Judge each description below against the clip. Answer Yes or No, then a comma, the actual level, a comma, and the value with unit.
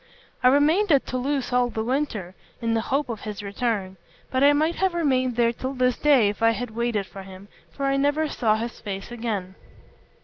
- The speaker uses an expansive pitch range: No, average, 4.1 semitones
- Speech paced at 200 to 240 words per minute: Yes, fast, 205 wpm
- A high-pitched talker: Yes, high, 245 Hz